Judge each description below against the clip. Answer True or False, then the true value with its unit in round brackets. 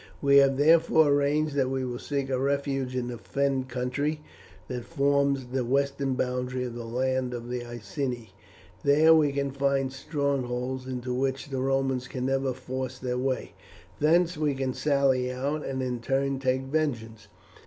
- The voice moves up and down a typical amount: False (1.8 semitones)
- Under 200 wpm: True (165 wpm)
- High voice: False (135 Hz)